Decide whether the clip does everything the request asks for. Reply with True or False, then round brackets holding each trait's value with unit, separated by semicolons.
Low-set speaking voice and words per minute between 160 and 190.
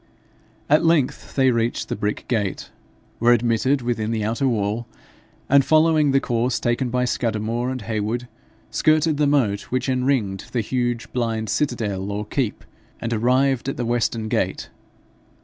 False (120 Hz; 150 wpm)